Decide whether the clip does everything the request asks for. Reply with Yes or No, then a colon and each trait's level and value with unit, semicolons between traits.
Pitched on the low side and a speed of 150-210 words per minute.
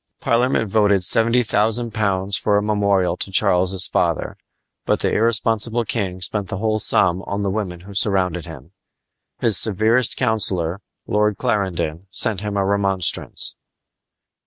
No: low, 100 Hz; average, 140 wpm